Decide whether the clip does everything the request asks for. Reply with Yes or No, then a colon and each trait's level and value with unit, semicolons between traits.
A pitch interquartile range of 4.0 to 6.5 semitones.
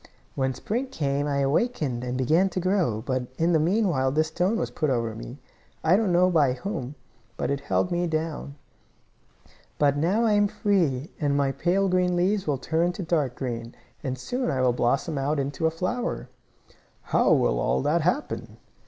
Yes: average, 5.3 semitones